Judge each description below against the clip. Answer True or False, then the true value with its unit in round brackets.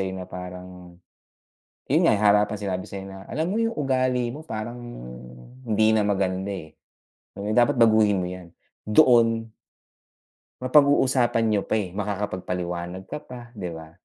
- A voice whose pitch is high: False (105 Hz)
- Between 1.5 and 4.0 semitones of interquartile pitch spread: False (4.4 semitones)